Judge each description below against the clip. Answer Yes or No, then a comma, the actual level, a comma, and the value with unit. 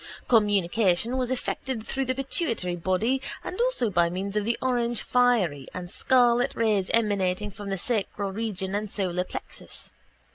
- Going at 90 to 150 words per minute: Yes, average, 145 wpm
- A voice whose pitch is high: Yes, high, 210 Hz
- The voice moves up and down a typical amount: Yes, average, 4.6 semitones